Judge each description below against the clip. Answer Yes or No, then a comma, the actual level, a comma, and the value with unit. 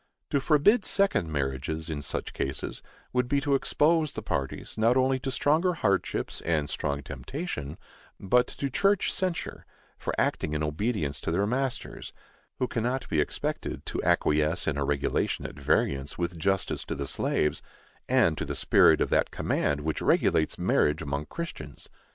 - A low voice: Yes, very low, 90 Hz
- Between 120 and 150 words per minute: No, average, 165 wpm